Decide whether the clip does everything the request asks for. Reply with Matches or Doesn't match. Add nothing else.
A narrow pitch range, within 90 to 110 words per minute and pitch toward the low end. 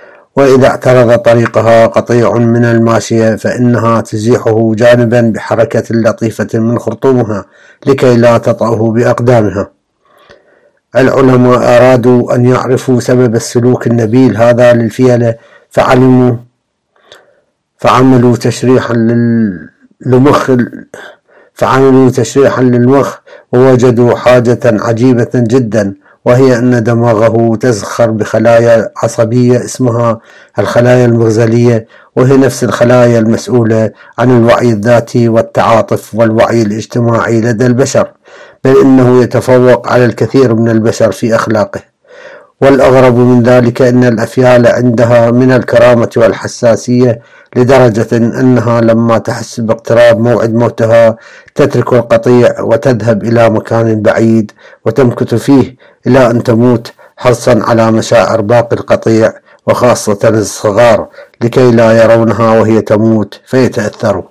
Matches